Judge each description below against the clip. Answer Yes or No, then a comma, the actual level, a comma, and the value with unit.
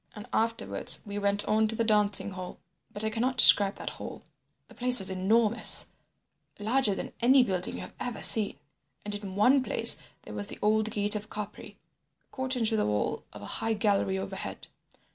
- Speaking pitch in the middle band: No, high, 210 Hz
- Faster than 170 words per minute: Yes, average, 180 wpm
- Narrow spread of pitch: Yes, narrow, 2.3 semitones